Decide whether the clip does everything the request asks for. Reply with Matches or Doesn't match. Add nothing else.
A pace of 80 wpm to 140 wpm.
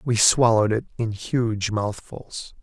Matches